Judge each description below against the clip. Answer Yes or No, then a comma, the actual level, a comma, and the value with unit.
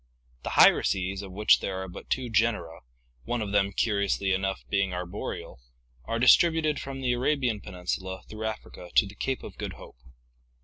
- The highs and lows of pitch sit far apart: No, average, 4.3 semitones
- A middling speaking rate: Yes, average, 175 wpm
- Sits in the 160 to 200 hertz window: No, low, 100 Hz